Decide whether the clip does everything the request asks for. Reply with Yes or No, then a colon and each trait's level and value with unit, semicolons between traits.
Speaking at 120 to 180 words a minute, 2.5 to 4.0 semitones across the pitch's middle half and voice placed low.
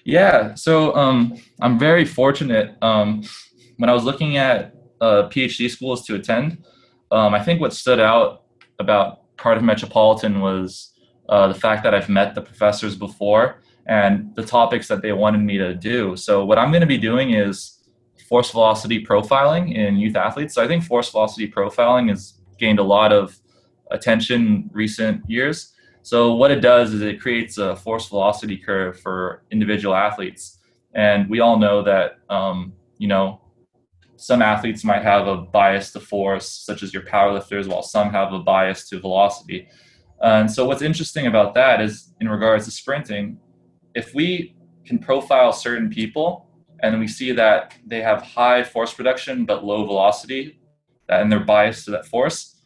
Yes: average, 170 wpm; average, 3.7 semitones; low, 110 Hz